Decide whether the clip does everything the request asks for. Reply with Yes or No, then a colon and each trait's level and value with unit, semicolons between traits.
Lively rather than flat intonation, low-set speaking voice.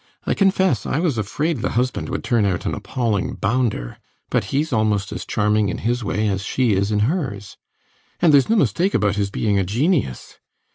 Yes: wide, 5.7 semitones; low, 110 Hz